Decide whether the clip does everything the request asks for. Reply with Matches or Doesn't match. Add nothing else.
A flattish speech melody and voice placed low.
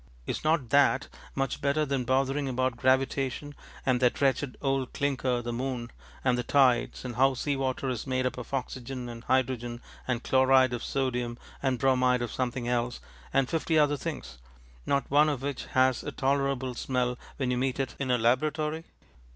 Matches